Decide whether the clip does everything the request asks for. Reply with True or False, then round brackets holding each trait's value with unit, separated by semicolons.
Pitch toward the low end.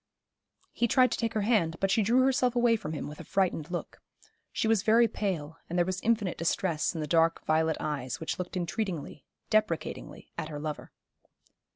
False (185 Hz)